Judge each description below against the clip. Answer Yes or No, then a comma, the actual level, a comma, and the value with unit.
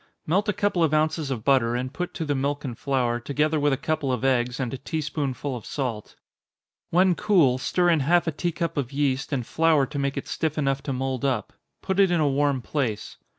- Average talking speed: No, fast, 235 wpm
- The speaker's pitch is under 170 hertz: Yes, medium, 140 Hz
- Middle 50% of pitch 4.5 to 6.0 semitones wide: No, average, 3.4 semitones